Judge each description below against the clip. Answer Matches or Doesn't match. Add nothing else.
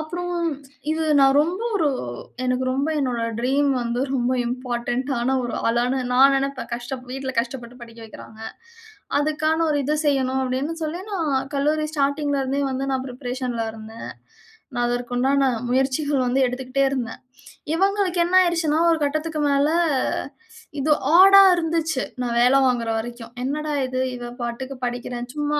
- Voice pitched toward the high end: Matches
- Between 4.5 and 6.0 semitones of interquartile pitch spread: Doesn't match